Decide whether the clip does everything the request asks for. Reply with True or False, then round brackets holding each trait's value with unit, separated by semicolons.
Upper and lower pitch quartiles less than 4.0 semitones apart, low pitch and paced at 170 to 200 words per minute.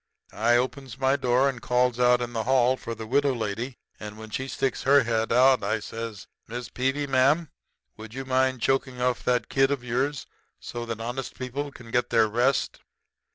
True (2.4 semitones; 125 Hz; 195 wpm)